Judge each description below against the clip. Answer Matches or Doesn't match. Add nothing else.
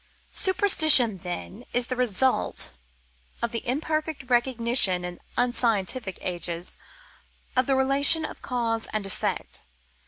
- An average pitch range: Matches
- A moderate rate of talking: Doesn't match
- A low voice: Doesn't match